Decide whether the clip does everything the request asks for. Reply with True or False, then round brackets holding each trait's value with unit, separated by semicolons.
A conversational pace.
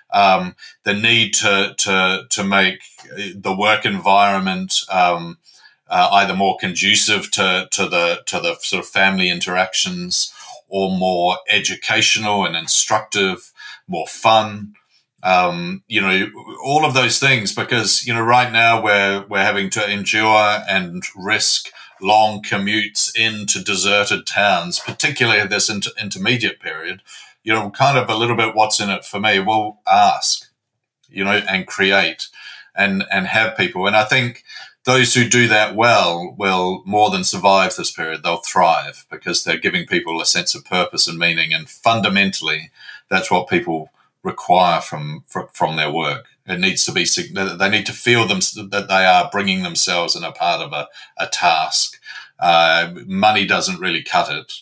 True (160 wpm)